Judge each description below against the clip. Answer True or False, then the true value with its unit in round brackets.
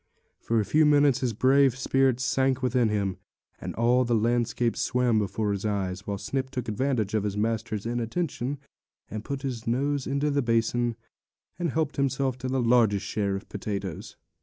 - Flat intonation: False (3.8 semitones)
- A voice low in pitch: True (120 Hz)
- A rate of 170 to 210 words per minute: True (180 wpm)